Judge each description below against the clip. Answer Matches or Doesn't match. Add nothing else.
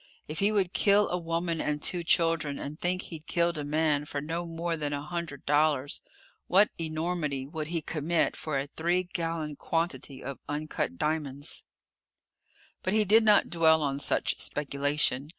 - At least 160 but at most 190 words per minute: Matches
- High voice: Doesn't match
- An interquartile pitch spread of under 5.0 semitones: Matches